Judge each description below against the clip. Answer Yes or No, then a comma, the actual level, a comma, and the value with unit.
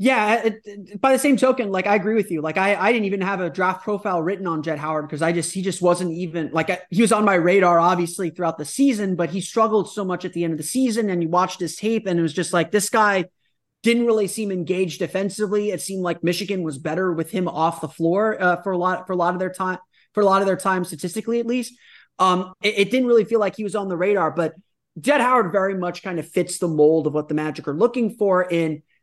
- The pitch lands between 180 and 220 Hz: Yes, medium, 185 Hz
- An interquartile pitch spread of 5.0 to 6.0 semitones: No, average, 3.3 semitones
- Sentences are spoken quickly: Yes, fast, 270 wpm